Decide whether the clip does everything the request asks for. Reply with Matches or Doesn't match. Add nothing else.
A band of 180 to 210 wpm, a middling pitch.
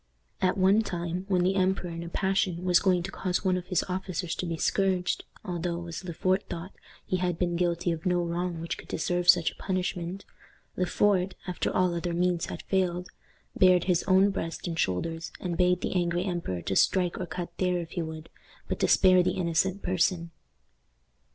Matches